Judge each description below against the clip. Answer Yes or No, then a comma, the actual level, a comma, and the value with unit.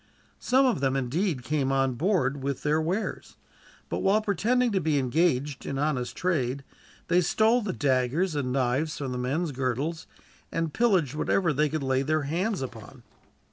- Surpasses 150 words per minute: Yes, average, 170 wpm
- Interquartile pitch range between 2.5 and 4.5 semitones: No, average, 5.1 semitones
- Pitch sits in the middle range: Yes, medium, 150 Hz